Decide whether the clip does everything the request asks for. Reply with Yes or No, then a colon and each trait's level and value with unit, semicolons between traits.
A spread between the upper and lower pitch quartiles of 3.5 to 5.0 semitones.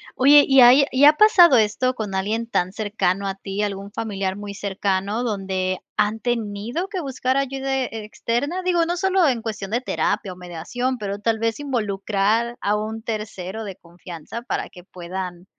Yes: average, 4.6 semitones